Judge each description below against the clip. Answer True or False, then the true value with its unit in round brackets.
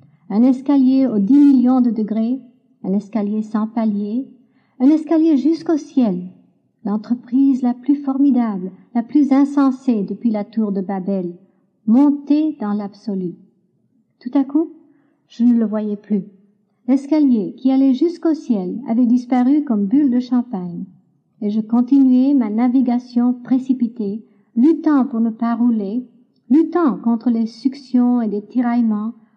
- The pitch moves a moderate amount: True (4.2 semitones)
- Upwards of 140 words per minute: False (135 wpm)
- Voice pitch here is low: False (240 Hz)